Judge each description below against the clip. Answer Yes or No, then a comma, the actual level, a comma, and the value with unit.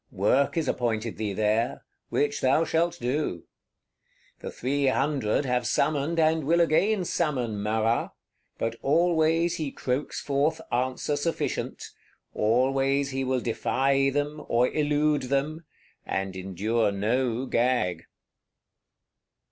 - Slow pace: Yes, slow, 115 wpm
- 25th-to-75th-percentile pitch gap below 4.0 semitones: No, average, 4.5 semitones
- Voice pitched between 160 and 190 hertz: No, low, 135 Hz